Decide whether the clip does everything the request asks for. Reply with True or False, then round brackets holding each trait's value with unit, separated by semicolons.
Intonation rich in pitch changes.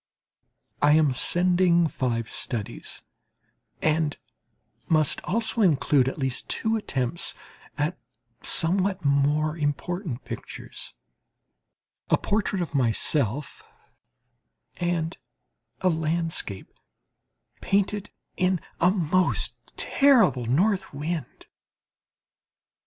False (4.6 semitones)